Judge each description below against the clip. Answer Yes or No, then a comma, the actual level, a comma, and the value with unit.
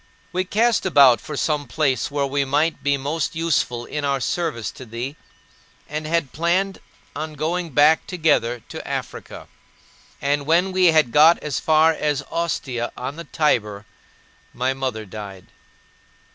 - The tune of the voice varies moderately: Yes, average, 4.1 semitones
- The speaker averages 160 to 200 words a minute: No, average, 150 wpm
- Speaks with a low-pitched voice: No, medium, 150 Hz